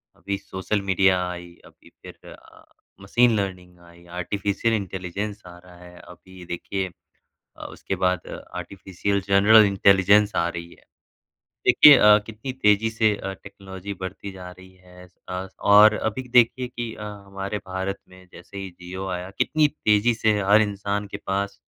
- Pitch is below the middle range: Yes, low, 100 Hz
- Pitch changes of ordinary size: No, narrow, 2.2 semitones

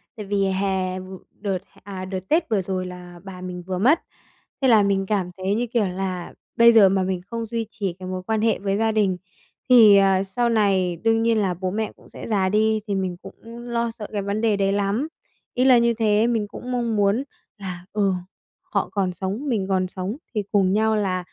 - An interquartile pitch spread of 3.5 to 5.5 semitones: No, average, 3.0 semitones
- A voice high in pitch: Yes, high, 200 Hz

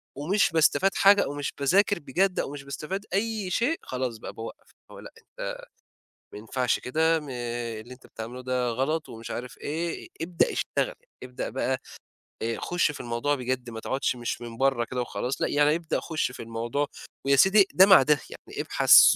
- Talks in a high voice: No, low, 135 Hz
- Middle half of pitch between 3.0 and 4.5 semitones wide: No, average, 5.1 semitones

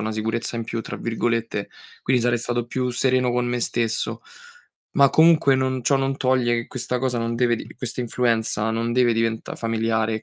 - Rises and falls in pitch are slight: Yes, narrow, 1.8 semitones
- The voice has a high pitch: No, low, 120 Hz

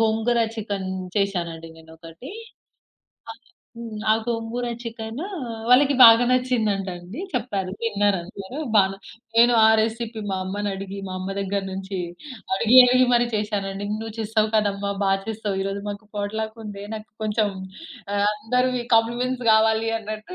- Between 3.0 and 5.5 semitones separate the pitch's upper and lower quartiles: No, narrow, 2.5 semitones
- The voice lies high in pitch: Yes, high, 215 Hz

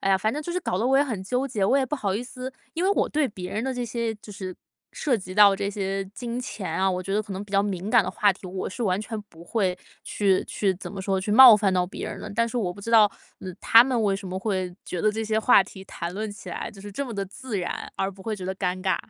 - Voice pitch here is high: Yes, high, 205 Hz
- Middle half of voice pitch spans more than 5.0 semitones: No, average, 3.4 semitones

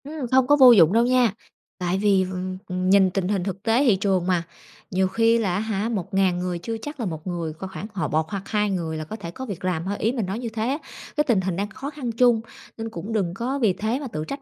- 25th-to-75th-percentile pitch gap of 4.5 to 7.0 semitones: No, average, 4.1 semitones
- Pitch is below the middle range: No, high, 200 Hz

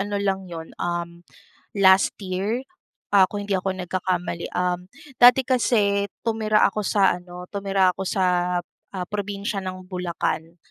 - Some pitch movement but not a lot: No, narrow, 2.0 semitones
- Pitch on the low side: No, high, 190 Hz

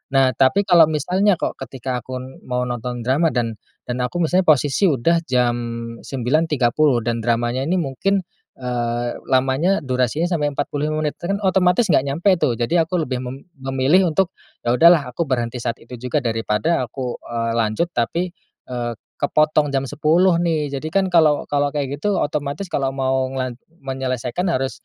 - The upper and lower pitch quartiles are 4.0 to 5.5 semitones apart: Yes, average, 4.8 semitones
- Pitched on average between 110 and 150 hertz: Yes, low, 135 Hz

